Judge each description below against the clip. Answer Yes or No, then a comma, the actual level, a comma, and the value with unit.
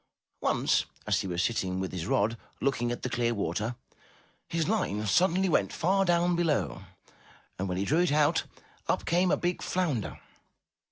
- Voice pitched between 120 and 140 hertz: Yes, low, 135 Hz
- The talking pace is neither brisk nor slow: Yes, average, 170 wpm